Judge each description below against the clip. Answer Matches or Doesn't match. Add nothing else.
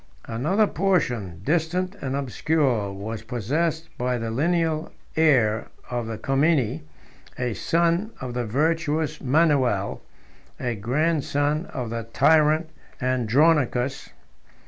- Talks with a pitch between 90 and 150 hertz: Matches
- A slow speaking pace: Matches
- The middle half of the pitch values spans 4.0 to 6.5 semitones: Matches